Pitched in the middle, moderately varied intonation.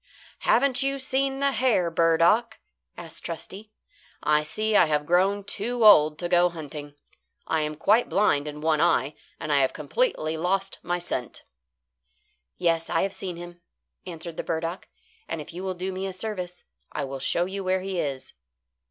Yes: medium, 175 Hz; average, 3.9 semitones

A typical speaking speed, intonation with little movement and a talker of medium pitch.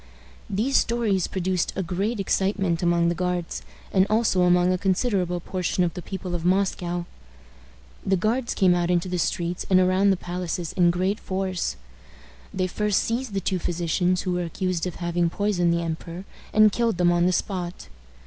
Yes: average, 175 wpm; narrow, 1.8 semitones; medium, 180 Hz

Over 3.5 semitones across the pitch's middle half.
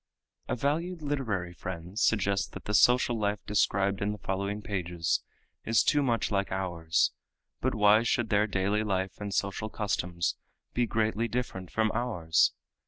No: average, 3.2 semitones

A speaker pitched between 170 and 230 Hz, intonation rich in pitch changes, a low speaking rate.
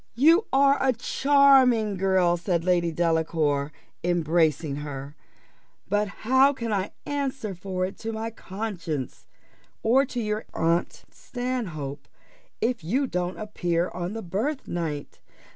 Yes: high, 190 Hz; wide, 6.4 semitones; slow, 125 wpm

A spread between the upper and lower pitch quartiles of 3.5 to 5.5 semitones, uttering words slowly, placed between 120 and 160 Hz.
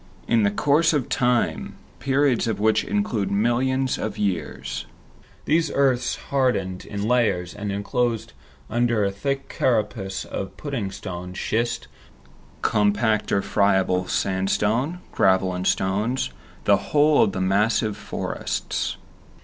No: average, 4.5 semitones; slow, 120 wpm; low, 110 Hz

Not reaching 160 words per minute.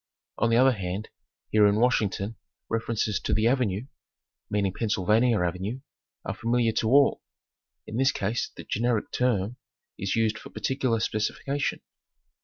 Yes: average, 140 wpm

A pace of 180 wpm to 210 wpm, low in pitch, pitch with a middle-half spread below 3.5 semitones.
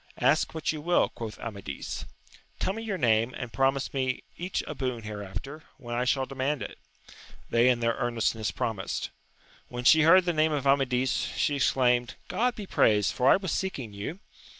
No: average, 185 wpm; low, 130 Hz; average, 4.8 semitones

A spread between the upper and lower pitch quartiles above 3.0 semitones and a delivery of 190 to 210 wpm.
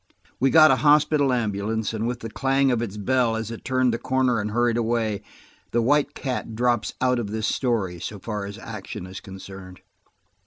Yes: average, 3.4 semitones; average, 195 wpm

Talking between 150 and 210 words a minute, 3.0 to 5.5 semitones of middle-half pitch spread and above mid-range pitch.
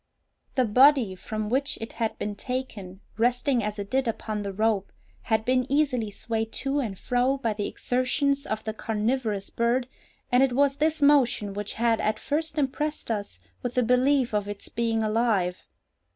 Yes: average, 175 wpm; average, 3.7 semitones; high, 235 Hz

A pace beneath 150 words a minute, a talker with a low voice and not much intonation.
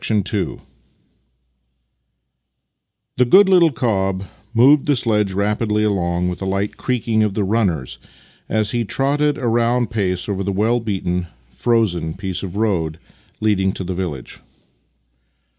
No: average, 140 wpm; low, 105 Hz; average, 3.9 semitones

